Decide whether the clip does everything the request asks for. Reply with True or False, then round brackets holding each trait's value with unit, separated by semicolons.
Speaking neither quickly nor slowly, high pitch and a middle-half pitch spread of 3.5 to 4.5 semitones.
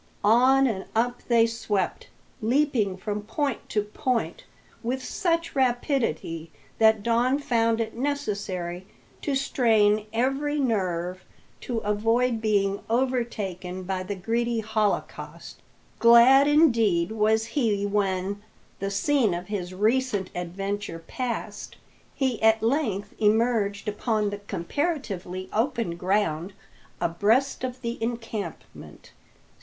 False (110 wpm; 220 Hz; 3.8 semitones)